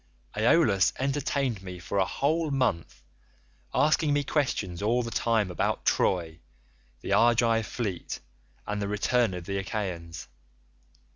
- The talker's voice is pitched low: Yes, low, 110 Hz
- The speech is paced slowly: Yes, slow, 130 wpm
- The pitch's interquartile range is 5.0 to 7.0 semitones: Yes, wide, 5.5 semitones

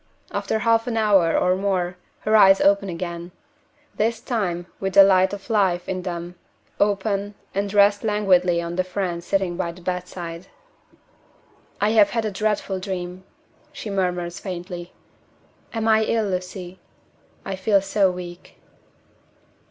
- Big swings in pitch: No, narrow, 2.4 semitones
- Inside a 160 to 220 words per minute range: No, average, 145 wpm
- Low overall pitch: No, high, 190 Hz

